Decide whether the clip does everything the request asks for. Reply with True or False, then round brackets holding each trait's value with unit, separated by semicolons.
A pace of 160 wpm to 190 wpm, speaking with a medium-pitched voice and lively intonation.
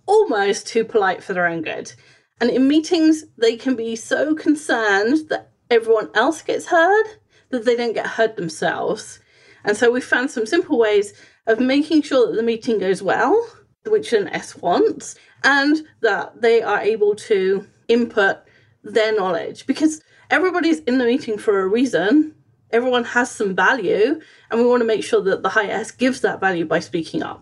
False (180 wpm; 255 Hz; 8.0 semitones)